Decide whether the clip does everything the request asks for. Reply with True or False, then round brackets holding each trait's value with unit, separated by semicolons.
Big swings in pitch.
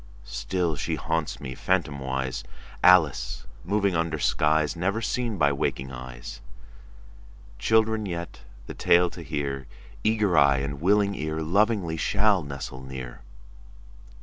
True (6.1 semitones)